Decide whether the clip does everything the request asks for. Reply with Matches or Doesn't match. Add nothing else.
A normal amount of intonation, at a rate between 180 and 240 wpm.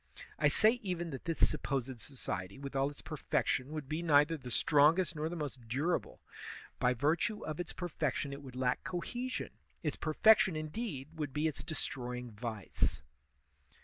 Doesn't match